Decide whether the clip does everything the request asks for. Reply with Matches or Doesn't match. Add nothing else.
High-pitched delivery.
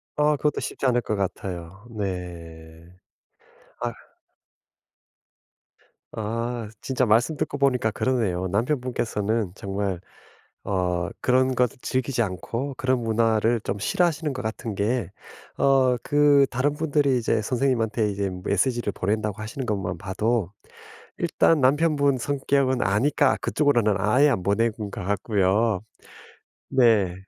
Doesn't match